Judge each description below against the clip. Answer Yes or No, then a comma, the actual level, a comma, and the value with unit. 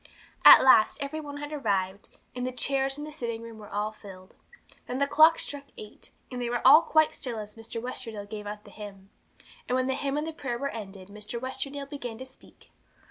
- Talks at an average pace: No, fast, 220 wpm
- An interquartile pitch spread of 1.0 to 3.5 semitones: No, average, 4.8 semitones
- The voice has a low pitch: No, high, 245 Hz